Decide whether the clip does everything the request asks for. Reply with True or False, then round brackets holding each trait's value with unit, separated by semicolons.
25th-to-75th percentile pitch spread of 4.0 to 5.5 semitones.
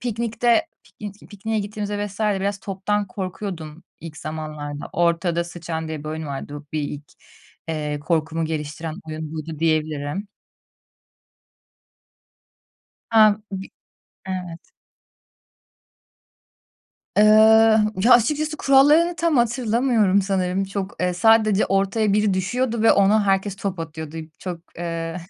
True (4.9 semitones)